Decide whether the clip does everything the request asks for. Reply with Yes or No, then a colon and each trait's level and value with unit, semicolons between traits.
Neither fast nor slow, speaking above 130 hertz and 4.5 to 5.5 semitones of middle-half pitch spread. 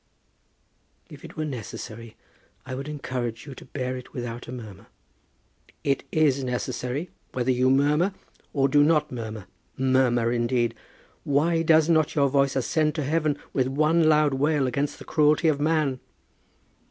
No: average, 155 wpm; medium, 140 Hz; average, 3.3 semitones